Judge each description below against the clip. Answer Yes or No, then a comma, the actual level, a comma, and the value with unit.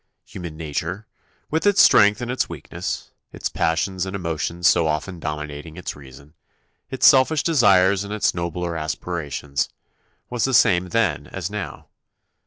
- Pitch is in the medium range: No, very low, 90 Hz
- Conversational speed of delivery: Yes, average, 145 wpm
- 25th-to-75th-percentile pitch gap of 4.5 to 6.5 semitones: Yes, average, 4.9 semitones